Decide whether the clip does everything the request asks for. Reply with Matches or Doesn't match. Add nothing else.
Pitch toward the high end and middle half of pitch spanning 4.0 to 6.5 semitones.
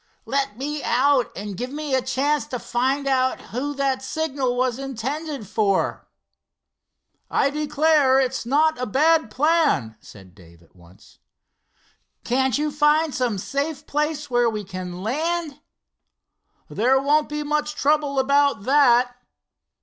Doesn't match